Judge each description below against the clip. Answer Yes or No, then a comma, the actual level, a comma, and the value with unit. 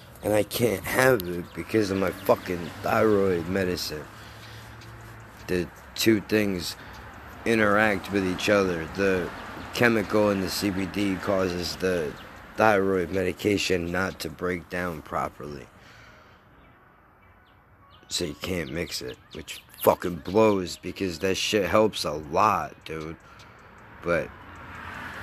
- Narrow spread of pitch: No, average, 3.3 semitones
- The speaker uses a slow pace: Yes, slow, 115 wpm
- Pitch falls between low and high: No, very low, 95 Hz